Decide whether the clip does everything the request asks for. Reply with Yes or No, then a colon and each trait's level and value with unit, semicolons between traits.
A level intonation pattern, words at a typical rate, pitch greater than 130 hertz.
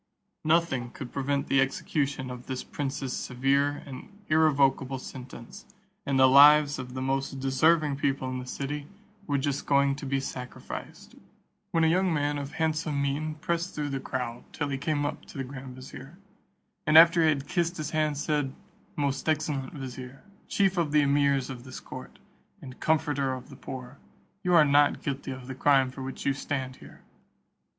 Yes: narrow, 2.3 semitones; average, 180 wpm; medium, 140 Hz